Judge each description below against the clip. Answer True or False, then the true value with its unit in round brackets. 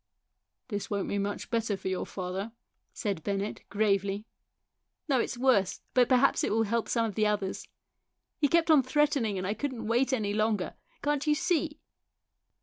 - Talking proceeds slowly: False (180 wpm)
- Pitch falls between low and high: False (220 Hz)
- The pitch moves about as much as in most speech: True (4.8 semitones)